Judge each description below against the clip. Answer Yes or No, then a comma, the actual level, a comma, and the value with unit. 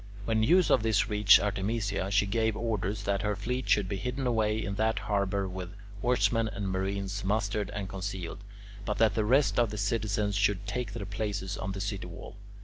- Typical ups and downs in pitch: No, narrow, 2.1 semitones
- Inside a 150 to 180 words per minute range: No, average, 195 wpm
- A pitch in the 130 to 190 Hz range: No, low, 105 Hz